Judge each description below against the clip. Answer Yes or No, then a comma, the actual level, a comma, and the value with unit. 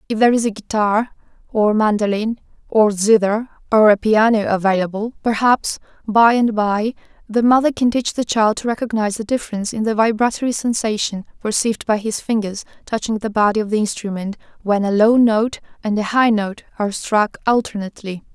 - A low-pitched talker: No, high, 215 Hz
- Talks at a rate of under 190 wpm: Yes, average, 170 wpm